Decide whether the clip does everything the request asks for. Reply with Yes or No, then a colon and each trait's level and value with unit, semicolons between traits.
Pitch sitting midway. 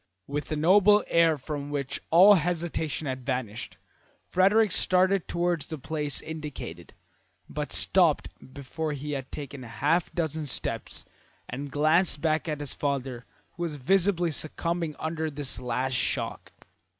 Yes: medium, 155 Hz